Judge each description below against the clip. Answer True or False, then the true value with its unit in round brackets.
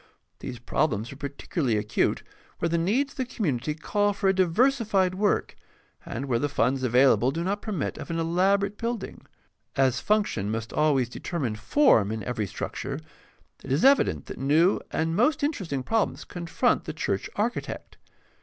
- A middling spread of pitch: False (8.1 semitones)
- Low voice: False (165 Hz)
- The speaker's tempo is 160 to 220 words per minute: True (165 wpm)